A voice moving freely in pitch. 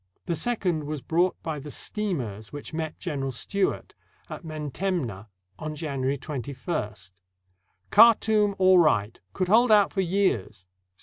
Yes: wide, 6.0 semitones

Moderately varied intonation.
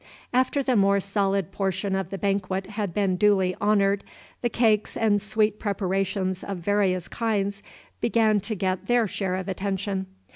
No: narrow, 1.7 semitones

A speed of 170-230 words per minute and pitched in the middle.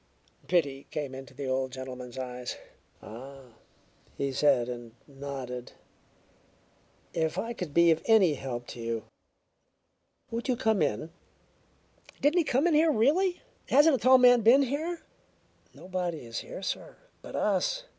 No: average, 145 wpm; medium, 155 Hz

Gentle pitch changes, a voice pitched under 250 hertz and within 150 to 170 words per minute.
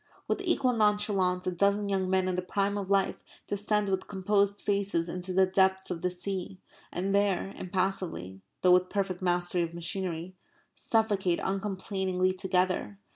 Yes: narrow, 1.7 semitones; high, 190 Hz; average, 155 wpm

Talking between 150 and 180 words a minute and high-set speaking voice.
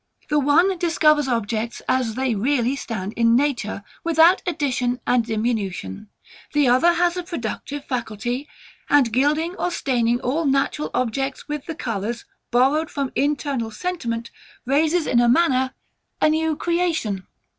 No: average, 140 wpm; very high, 265 Hz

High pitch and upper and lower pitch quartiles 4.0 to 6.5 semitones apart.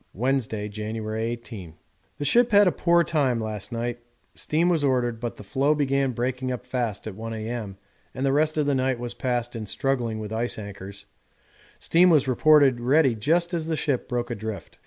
No: low, 125 Hz; average, 4.3 semitones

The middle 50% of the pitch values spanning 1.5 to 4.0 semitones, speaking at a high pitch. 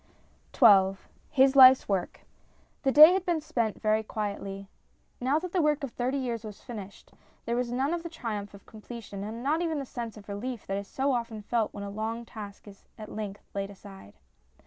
No: average, 4.7 semitones; high, 230 Hz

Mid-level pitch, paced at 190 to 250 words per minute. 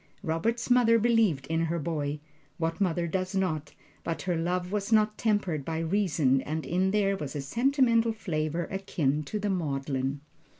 No: medium, 175 Hz; average, 170 wpm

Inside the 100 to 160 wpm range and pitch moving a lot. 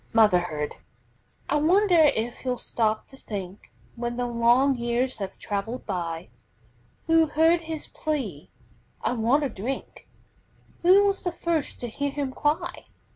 Yes: average, 140 wpm; wide, 6.0 semitones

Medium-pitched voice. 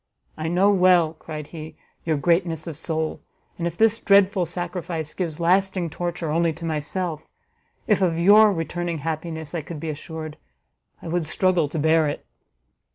Yes: medium, 165 Hz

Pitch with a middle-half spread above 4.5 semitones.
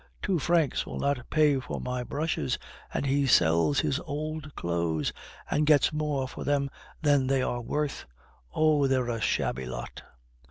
No: average, 3.4 semitones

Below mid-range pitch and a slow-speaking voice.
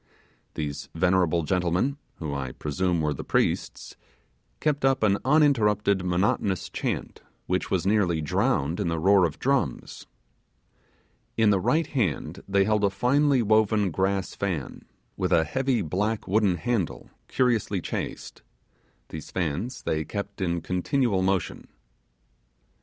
Yes: very low, 95 Hz; slow, 130 wpm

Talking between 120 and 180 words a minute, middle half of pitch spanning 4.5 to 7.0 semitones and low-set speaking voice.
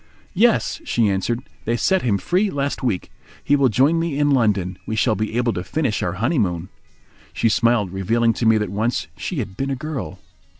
No: average, 200 wpm; average, 5.3 semitones; low, 120 Hz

